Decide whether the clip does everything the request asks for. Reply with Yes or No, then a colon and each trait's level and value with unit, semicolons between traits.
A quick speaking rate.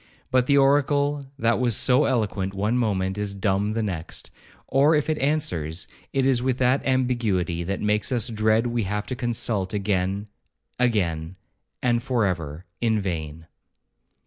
No: average, 145 wpm